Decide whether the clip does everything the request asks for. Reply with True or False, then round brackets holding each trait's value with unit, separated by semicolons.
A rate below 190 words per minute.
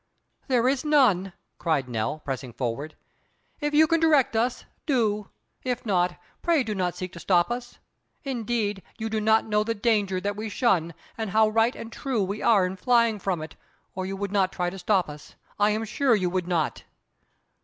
False (195 wpm)